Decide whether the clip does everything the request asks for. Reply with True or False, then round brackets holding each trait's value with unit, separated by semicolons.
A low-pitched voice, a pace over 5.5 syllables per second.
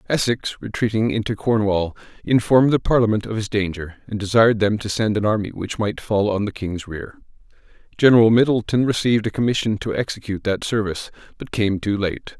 True (110 Hz; 5.8 syllables/s)